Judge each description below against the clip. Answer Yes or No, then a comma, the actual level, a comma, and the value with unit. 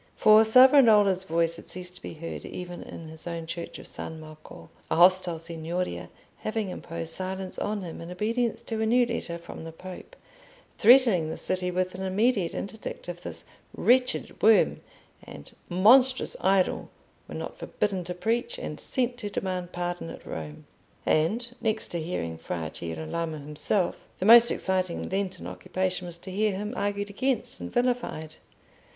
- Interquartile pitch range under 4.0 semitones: No, average, 4.5 semitones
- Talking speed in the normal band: Yes, average, 165 wpm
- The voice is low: No, medium, 185 Hz